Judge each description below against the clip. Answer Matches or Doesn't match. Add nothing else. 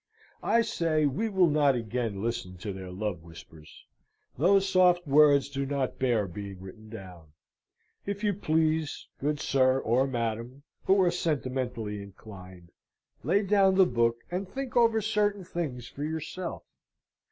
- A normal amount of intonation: Doesn't match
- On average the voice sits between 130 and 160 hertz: Matches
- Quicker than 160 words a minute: Doesn't match